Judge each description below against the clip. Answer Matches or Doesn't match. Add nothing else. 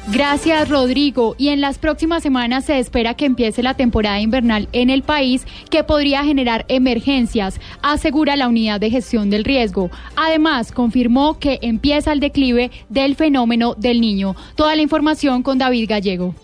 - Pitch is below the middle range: Doesn't match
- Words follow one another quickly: Doesn't match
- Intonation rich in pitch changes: Doesn't match